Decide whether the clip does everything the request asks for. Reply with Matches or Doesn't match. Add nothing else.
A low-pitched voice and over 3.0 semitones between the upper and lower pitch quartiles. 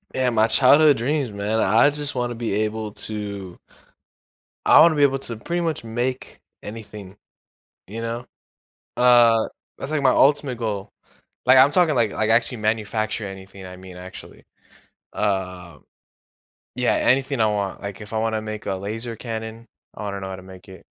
Matches